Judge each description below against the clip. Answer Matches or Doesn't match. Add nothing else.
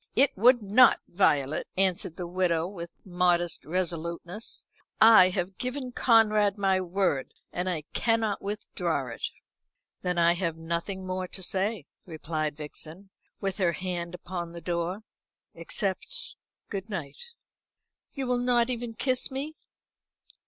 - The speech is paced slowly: Matches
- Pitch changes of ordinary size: Matches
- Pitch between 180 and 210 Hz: Matches